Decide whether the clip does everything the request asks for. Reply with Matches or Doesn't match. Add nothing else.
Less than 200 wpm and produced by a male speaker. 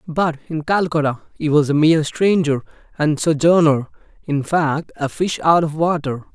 Matches